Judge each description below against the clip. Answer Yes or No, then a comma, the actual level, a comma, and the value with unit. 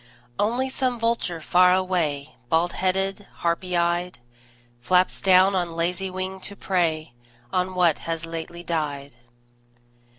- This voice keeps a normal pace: No, slow, 125 wpm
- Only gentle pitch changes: Yes, narrow, 2.3 semitones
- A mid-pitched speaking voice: Yes, medium, 180 Hz